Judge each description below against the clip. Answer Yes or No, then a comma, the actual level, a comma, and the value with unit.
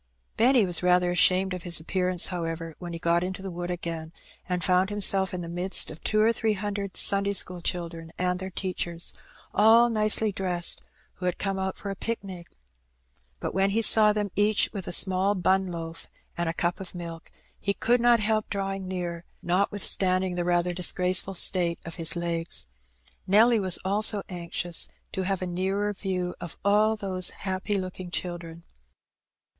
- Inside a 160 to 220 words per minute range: Yes, average, 180 wpm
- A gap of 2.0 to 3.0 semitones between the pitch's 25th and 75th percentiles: Yes, narrow, 2.4 semitones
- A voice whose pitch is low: No, medium, 185 Hz